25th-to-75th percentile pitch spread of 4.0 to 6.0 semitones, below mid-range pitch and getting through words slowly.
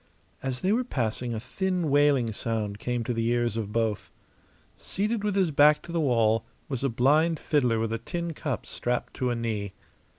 No: wide, 5.4 semitones; low, 125 Hz; average, 195 wpm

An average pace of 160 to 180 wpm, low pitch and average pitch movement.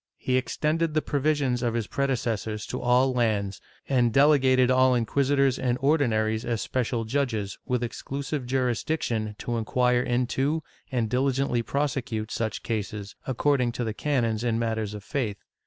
No: average, 150 wpm; low, 125 Hz; average, 3.3 semitones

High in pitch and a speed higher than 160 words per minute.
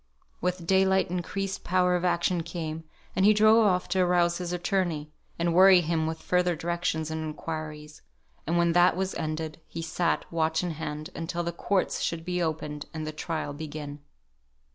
No: medium, 170 Hz; average, 175 wpm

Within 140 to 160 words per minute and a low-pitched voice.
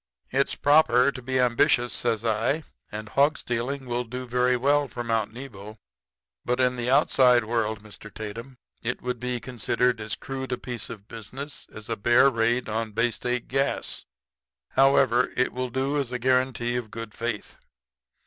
No: average, 170 wpm; low, 125 Hz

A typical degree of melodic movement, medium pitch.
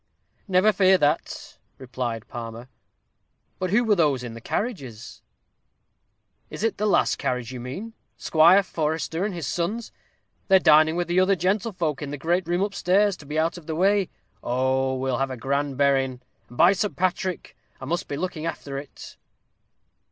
No: wide, 5.8 semitones; medium, 160 Hz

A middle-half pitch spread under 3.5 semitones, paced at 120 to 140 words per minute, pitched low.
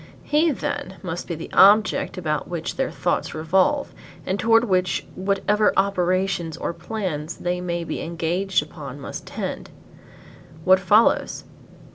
No: average, 2.9 semitones; slow, 135 wpm; medium, 185 Hz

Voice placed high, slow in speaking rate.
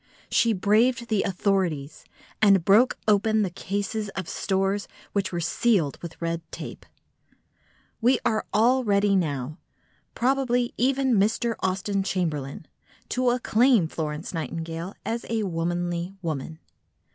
Yes: high, 195 Hz; slow, 115 wpm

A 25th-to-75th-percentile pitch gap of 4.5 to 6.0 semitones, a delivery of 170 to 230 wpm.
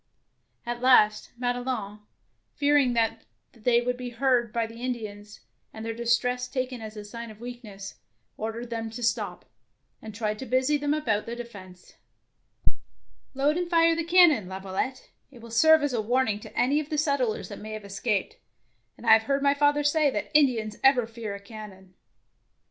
No: average, 3.7 semitones; average, 180 wpm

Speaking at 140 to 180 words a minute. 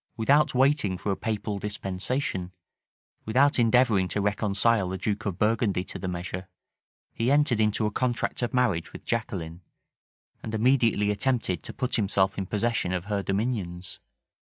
Yes: average, 150 wpm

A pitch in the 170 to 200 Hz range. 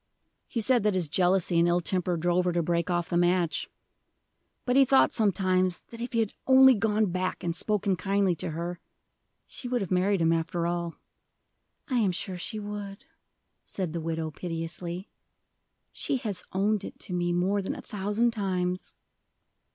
Yes: medium, 185 Hz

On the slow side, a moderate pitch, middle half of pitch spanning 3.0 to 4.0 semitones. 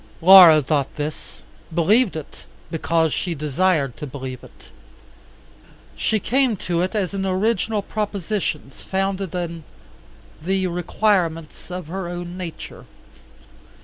Yes: slow, 115 wpm; medium, 175 Hz; average, 3.4 semitones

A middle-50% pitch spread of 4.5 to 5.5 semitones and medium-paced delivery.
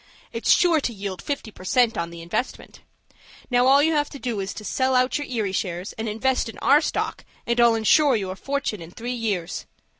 No: average, 5.0 semitones; fast, 220 wpm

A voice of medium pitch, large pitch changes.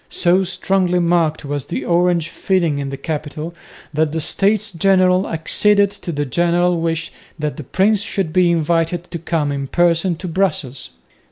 No: medium, 170 Hz; average, 3.0 semitones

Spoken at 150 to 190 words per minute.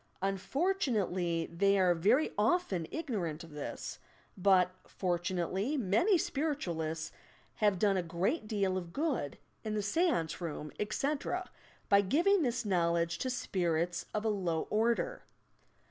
No: slow, 135 wpm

